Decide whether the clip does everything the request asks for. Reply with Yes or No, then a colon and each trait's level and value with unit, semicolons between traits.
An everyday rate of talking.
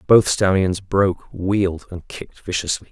Yes: average, 145 wpm